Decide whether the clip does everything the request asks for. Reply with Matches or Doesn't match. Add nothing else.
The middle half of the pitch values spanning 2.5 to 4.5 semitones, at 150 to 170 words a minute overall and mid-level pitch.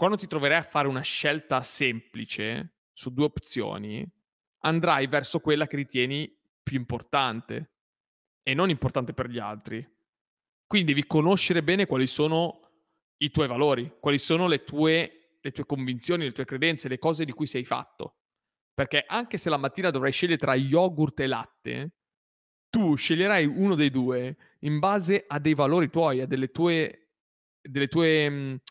Matches